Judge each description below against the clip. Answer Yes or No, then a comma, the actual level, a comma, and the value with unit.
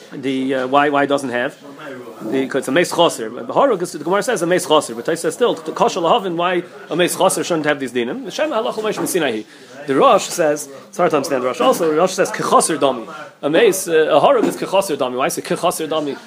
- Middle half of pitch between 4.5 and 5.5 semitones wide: Yes, average, 4.8 semitones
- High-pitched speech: No, medium, 155 Hz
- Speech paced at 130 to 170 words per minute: No, fast, 205 wpm